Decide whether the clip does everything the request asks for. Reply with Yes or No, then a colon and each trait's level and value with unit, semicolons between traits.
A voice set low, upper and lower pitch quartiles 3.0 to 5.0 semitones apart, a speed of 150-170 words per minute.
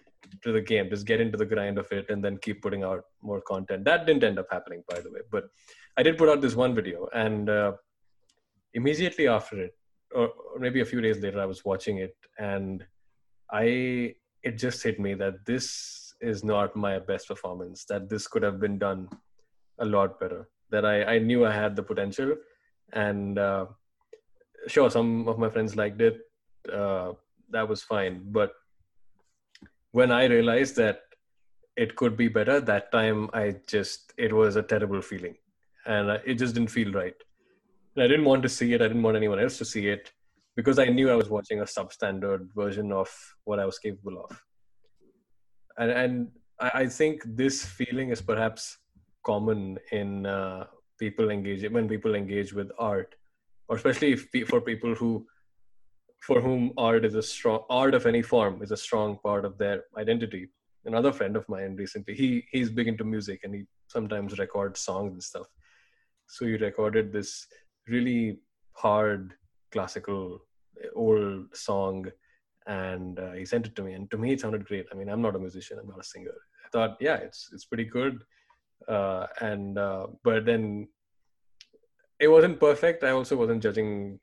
No: low, 110 Hz; average, 3.7 semitones; average, 180 wpm